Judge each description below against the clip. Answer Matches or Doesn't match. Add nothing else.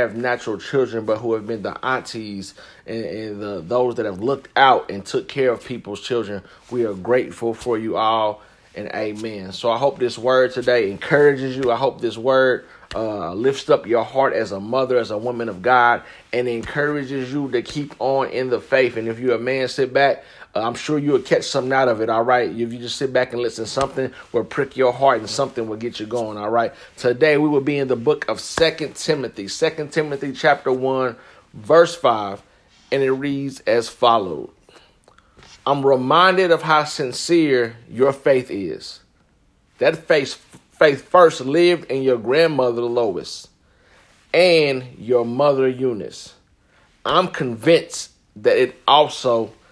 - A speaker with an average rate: Matches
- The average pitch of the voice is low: Matches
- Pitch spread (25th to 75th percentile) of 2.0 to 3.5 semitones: Matches